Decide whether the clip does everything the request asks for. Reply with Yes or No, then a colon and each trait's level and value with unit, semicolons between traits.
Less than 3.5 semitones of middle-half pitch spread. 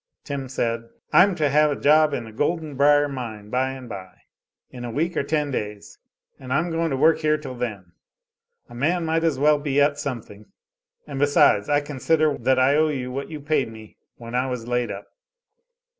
No: average, 3.8 semitones